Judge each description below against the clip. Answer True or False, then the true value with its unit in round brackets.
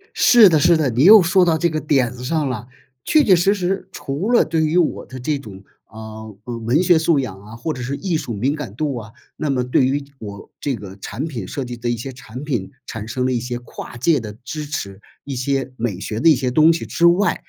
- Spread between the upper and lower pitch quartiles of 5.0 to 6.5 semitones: True (5.3 semitones)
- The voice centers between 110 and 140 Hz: True (135 Hz)